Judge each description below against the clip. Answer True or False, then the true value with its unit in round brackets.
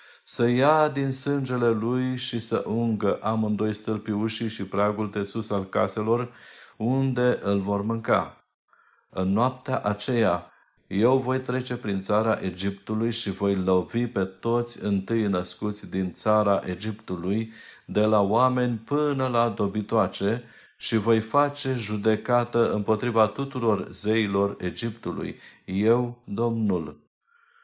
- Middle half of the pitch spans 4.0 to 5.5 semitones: False (3.2 semitones)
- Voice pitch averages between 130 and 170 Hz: False (110 Hz)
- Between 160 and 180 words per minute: False (120 wpm)